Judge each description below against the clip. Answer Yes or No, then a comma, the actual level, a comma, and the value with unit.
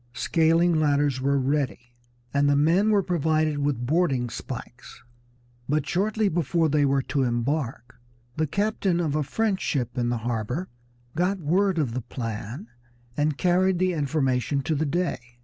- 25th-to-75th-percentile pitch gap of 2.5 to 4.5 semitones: No, average, 5.1 semitones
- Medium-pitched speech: Yes, medium, 150 Hz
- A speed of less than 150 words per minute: No, average, 155 wpm